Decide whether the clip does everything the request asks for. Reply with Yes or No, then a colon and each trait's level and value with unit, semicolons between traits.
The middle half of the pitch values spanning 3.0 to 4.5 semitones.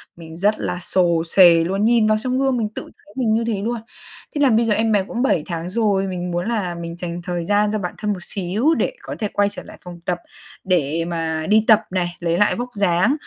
Yes: average, 3.9 semitones